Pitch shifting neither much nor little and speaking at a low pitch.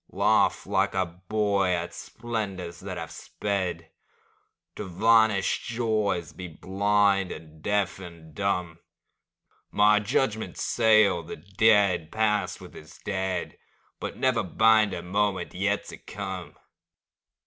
Yes: average, 3.0 semitones; low, 100 Hz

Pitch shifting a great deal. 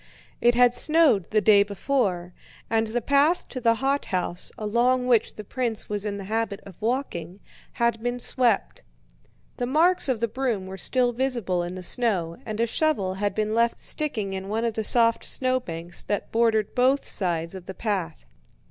No: average, 4.2 semitones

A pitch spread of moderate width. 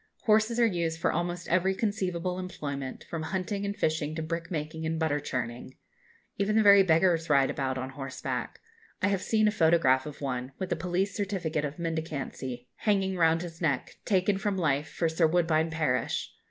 Yes: average, 4.2 semitones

